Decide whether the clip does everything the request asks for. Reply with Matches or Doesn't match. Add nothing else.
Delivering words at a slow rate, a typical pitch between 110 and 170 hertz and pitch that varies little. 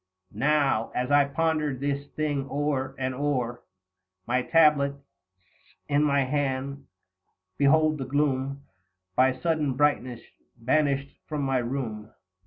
Matches